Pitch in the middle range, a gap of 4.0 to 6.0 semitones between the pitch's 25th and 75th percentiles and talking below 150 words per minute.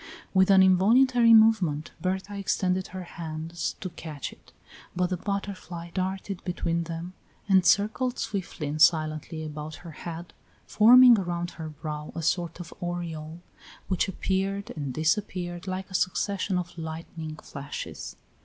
No: medium, 175 Hz; average, 3.1 semitones; average, 140 wpm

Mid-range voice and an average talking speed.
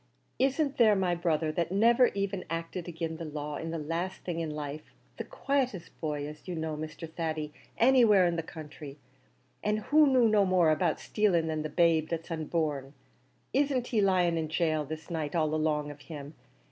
Yes: medium, 165 Hz; average, 185 wpm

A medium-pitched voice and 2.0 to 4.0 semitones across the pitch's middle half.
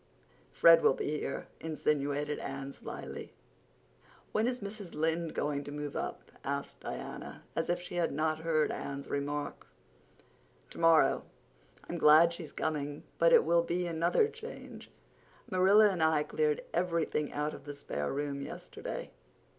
Yes: medium, 160 Hz; average, 2.9 semitones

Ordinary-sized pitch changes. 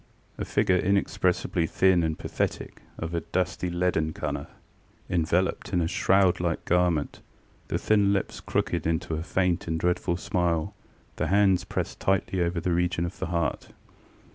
No: narrow, 1.9 semitones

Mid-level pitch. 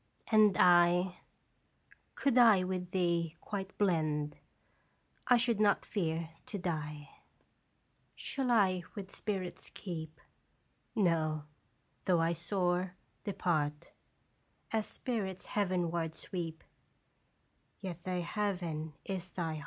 Yes: medium, 180 Hz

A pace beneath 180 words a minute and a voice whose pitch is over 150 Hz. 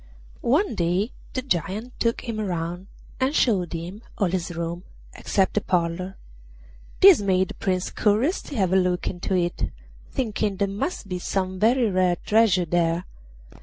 Yes: average, 160 wpm; high, 190 Hz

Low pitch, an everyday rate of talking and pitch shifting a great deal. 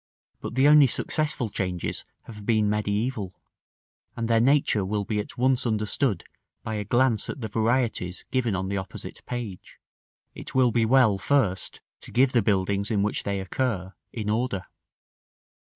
No: low, 110 Hz; average, 160 wpm; average, 3.9 semitones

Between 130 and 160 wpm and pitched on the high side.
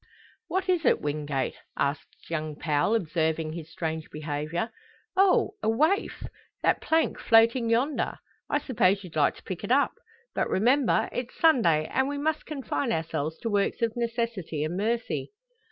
Yes: average, 155 wpm; high, 210 Hz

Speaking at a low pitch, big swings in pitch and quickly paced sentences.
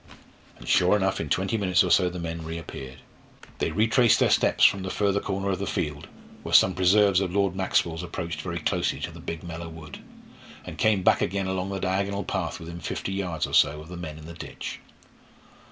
No: very low, 90 Hz; average, 2.9 semitones; fast, 210 wpm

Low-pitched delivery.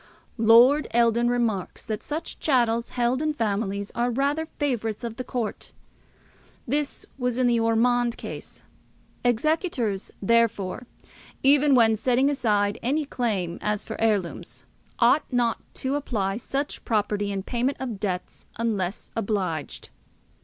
No: high, 235 Hz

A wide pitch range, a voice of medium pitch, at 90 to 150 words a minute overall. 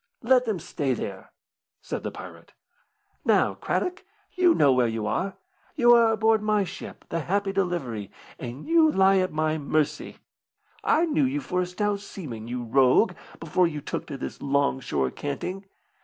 No: wide, 7.9 semitones; medium, 180 Hz; average, 170 wpm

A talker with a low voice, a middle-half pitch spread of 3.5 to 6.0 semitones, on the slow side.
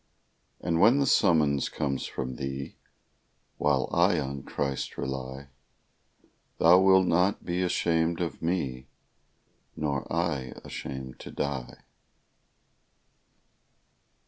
Yes: very low, 75 Hz; average, 4.4 semitones; slow, 100 wpm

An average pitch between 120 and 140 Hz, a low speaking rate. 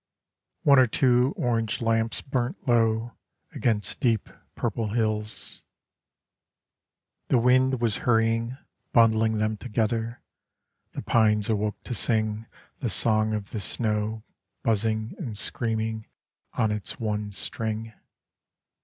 No: low, 110 Hz; slow, 110 wpm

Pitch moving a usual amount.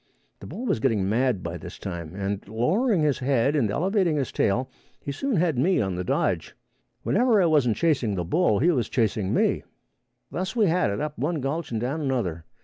No: wide, 8.3 semitones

